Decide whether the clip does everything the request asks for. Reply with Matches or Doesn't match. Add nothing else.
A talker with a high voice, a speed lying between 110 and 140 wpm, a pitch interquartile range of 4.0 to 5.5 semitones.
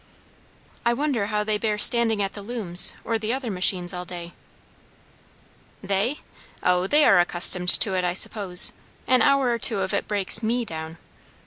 Doesn't match